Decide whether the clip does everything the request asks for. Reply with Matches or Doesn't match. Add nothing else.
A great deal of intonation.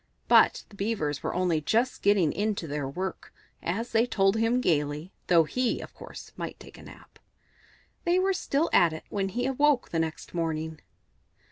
Matches